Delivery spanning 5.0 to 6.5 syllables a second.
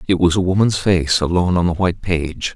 Yes: 5.9 syllables/s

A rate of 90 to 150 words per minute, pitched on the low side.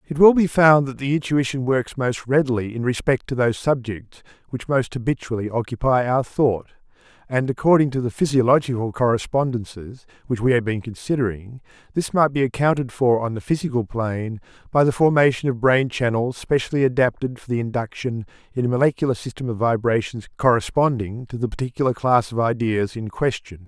No: average, 170 wpm; low, 125 Hz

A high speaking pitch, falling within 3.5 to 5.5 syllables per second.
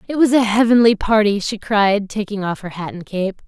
Yes: high, 210 Hz; 5.2 syllables/s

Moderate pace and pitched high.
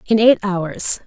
Yes: average, 170 wpm; high, 200 Hz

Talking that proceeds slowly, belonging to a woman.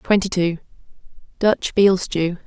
Yes: slow, 95 wpm; female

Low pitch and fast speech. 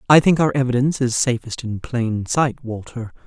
No: low, 125 Hz; average, 185 wpm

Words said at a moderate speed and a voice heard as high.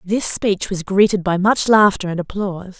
Yes: average, 195 wpm; high, 195 Hz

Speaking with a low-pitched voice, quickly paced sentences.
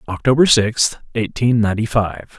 No: low, 115 Hz; slow, 125 wpm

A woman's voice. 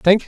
No: male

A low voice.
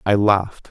Yes: low, 100 Hz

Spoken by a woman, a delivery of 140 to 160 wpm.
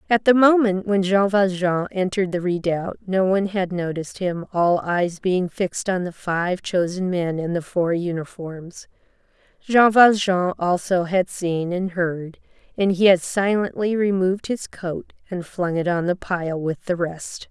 No: female; average, 170 wpm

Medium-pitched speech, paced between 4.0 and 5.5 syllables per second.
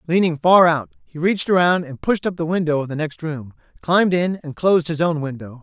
No: medium, 165 Hz; 5.7 syllables/s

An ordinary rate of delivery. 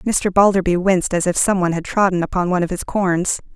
No: fast, 235 wpm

